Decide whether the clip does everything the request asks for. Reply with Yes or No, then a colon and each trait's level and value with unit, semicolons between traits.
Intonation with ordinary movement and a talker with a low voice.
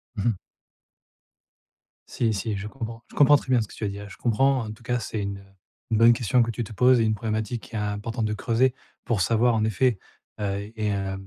No: narrow, 2.3 semitones; low, 110 Hz